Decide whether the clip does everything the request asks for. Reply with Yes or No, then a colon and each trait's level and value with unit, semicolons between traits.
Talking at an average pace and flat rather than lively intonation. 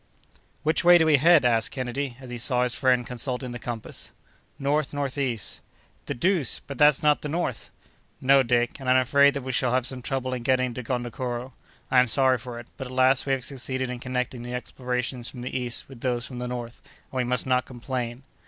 No: fast, 220 wpm; narrow, 1.6 semitones